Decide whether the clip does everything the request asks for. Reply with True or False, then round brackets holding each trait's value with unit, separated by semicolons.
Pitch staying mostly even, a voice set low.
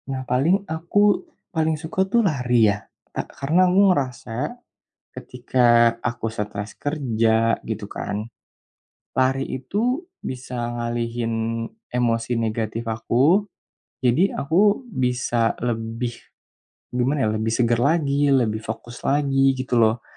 False (4.1 semitones; 125 Hz)